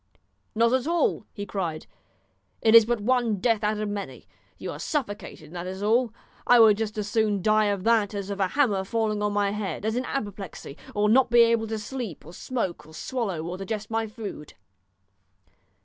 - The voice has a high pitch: Yes, high, 215 Hz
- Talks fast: Yes, fast, 210 wpm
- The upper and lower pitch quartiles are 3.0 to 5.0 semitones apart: No, narrow, 2.5 semitones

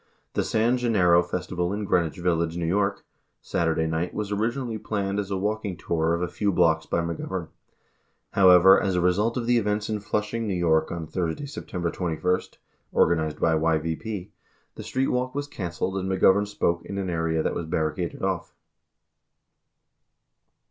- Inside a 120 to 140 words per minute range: No, average, 165 wpm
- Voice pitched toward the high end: No, very low, 90 Hz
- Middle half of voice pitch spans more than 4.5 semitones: No, average, 3.7 semitones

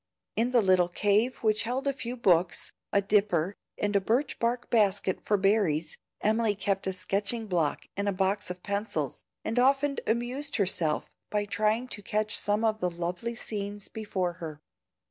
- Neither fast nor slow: Yes, average, 170 wpm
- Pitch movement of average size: Yes, average, 3.5 semitones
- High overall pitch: Yes, high, 205 Hz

